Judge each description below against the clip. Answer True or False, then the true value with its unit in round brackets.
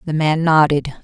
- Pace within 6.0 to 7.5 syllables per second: False (4.5 syllables/s)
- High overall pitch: False (155 Hz)